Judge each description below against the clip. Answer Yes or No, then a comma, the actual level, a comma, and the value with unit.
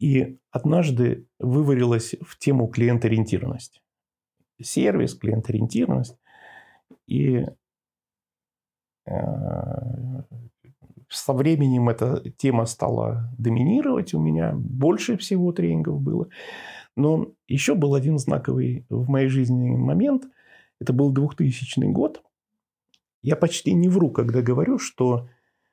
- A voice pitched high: No, low, 130 Hz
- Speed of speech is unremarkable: No, slow, 95 wpm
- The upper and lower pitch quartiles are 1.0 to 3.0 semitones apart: No, average, 3.5 semitones